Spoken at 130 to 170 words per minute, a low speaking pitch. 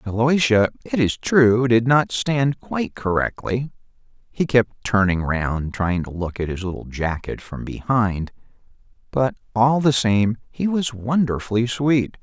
Yes: average, 145 wpm; low, 115 Hz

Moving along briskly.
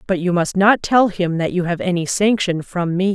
Yes: fast, 250 wpm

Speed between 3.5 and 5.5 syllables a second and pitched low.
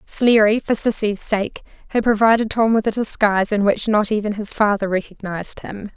No: 5.3 syllables/s; high, 210 Hz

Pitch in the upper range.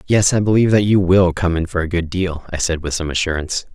No: very low, 90 Hz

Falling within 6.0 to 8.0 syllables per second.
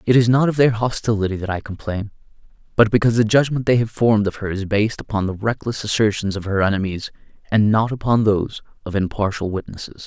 Yes: 6.3 syllables/s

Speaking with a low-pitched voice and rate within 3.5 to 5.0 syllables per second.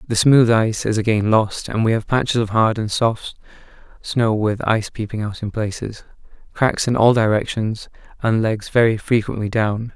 Yes: low, 110 Hz; 4.9 syllables/s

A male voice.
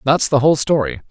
Yes: male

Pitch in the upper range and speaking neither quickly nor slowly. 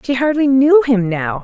No: high, 245 Hz; fast, 210 wpm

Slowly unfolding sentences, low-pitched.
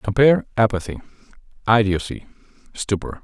Yes: slow, 75 wpm; low, 110 Hz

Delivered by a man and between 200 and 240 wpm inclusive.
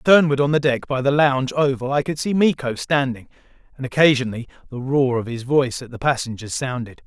Yes: male; fast, 205 wpm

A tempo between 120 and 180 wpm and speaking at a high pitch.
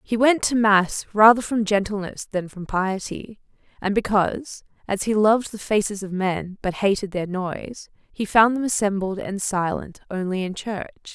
Yes: average, 170 wpm; high, 205 Hz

